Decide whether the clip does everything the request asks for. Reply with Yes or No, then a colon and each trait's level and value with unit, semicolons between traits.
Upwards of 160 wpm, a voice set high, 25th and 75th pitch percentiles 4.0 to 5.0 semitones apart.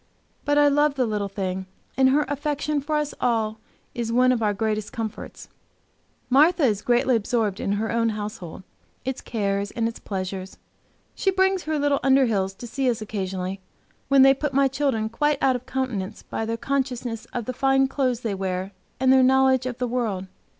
Yes: average, 185 wpm; high, 245 Hz; average, 4.3 semitones